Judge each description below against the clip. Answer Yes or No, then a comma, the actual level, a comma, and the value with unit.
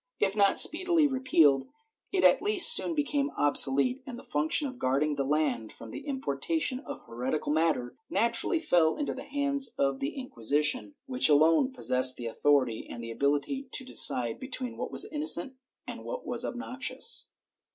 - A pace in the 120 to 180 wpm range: Yes, average, 165 wpm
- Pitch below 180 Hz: No, high, 210 Hz